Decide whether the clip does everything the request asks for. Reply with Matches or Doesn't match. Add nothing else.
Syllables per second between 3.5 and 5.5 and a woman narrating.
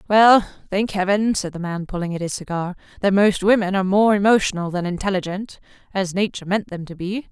Doesn't match